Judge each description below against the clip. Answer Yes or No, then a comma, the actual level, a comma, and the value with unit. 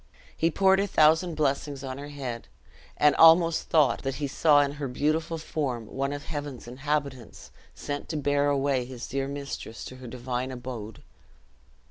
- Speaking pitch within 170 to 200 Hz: No, medium, 140 Hz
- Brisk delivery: No, average, 165 wpm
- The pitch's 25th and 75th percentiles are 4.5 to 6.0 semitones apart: No, average, 2.7 semitones